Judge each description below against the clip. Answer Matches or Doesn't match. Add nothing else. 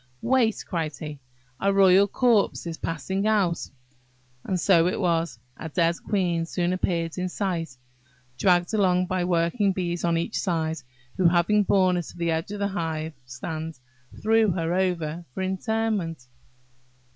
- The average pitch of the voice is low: Doesn't match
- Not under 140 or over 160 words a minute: Matches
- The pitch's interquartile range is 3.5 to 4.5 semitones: Doesn't match